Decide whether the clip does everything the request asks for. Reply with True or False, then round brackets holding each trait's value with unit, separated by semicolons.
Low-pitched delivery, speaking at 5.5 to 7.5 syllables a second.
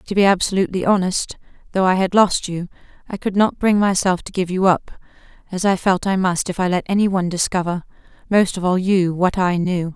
False (185 Hz; 5.7 syllables/s)